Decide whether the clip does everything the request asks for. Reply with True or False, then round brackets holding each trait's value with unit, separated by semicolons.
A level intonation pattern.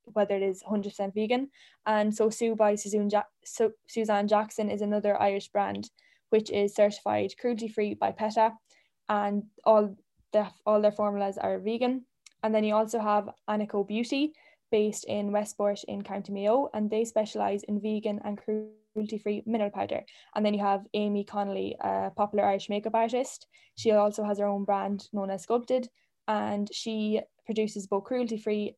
True (1.3 semitones)